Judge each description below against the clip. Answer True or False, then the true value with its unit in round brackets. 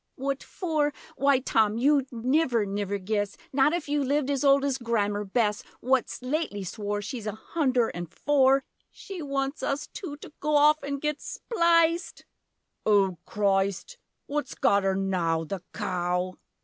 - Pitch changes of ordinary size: False (6.2 semitones)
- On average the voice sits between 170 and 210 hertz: False (255 Hz)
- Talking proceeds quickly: False (155 wpm)